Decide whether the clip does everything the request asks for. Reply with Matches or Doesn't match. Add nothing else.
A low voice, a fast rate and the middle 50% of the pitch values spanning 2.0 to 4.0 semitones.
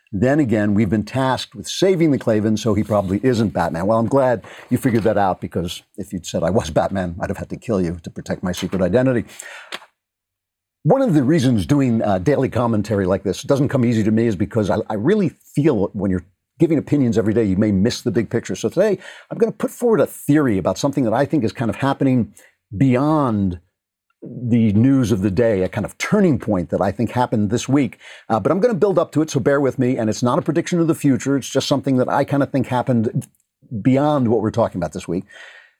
Doesn't match